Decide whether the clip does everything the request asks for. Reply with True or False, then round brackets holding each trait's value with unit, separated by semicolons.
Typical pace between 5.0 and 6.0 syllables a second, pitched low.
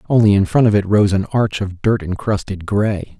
True (5.1 syllables/s; 100 Hz)